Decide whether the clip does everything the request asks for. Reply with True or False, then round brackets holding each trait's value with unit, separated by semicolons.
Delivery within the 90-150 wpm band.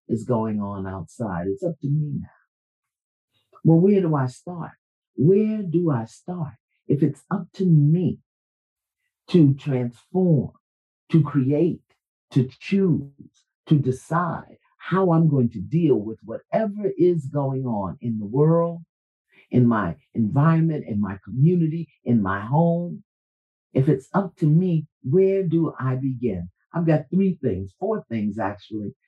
True (140 wpm)